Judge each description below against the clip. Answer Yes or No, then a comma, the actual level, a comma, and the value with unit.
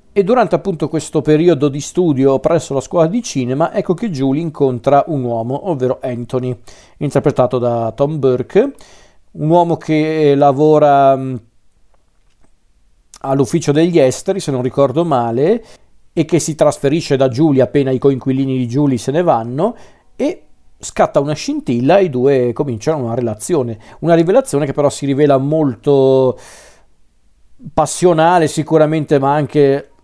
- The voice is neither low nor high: Yes, medium, 145 Hz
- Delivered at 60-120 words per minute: No, average, 140 wpm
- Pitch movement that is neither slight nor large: Yes, average, 3.5 semitones